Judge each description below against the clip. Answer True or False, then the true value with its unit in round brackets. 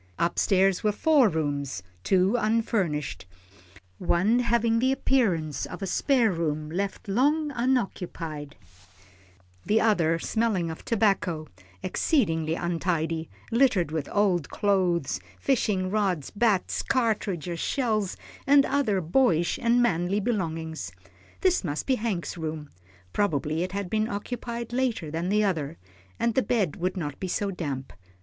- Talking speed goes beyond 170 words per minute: False (135 wpm)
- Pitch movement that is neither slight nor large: False (5.9 semitones)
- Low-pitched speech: False (190 Hz)